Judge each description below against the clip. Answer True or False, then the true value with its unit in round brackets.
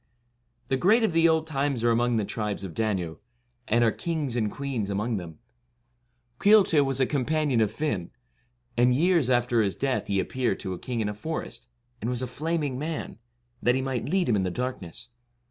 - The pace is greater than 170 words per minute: True (200 wpm)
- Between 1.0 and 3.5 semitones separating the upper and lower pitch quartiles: False (5.4 semitones)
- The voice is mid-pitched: False (125 Hz)